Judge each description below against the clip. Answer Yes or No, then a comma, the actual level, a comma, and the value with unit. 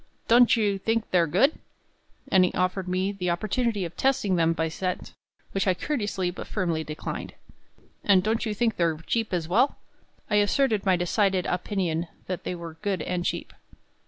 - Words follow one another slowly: No, average, 175 wpm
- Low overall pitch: No, high, 190 Hz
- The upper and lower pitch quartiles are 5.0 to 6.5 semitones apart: No, average, 3.4 semitones